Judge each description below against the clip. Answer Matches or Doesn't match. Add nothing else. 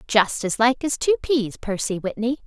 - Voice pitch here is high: Matches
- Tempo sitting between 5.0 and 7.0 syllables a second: Doesn't match